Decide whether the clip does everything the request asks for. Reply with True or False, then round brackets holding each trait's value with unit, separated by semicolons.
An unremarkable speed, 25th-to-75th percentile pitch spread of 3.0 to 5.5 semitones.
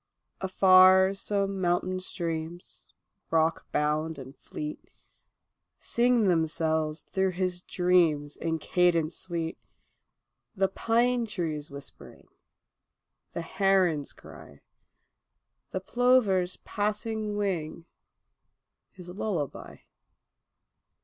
False (80 wpm; 3.3 semitones)